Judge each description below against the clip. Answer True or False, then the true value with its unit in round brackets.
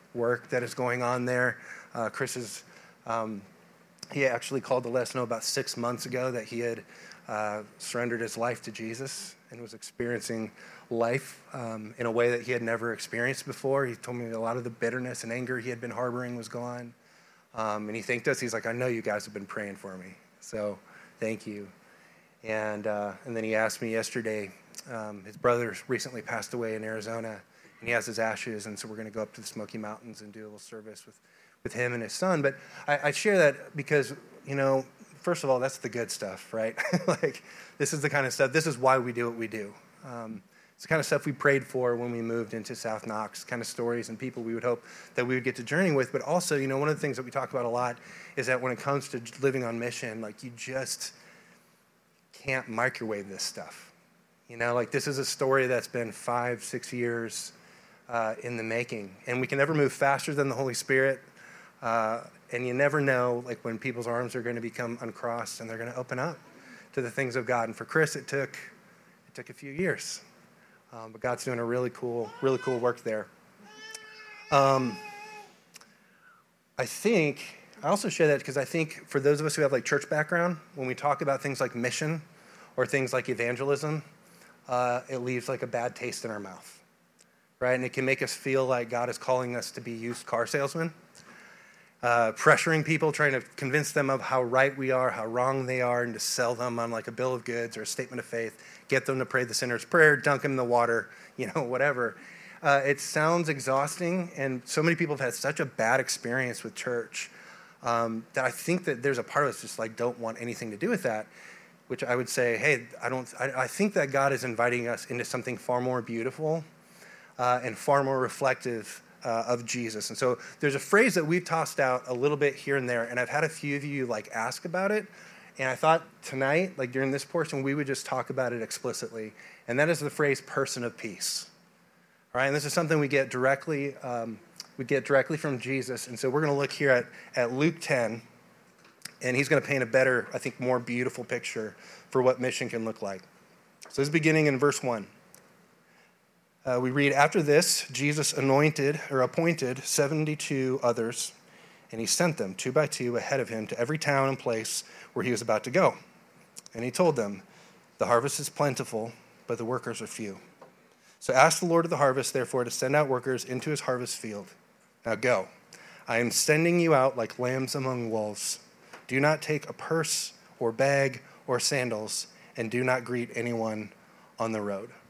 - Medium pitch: False (125 Hz)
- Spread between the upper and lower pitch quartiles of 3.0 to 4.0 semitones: True (3.3 semitones)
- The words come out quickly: True (220 wpm)